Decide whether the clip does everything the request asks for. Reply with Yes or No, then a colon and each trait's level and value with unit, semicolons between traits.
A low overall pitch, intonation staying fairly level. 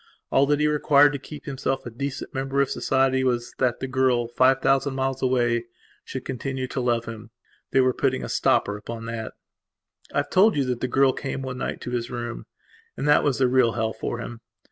Yes: low, 130 Hz; narrow, 2.2 semitones